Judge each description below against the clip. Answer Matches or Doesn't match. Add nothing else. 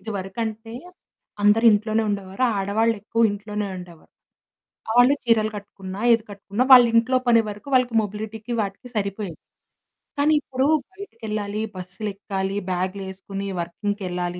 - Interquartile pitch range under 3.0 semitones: Matches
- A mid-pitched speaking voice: Doesn't match